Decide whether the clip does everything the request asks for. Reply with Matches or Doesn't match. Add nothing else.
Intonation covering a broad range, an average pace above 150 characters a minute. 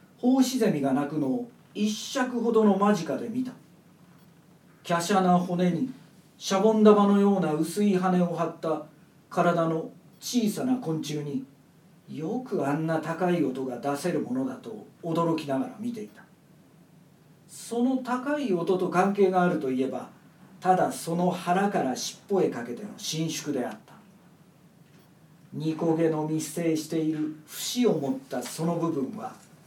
Doesn't match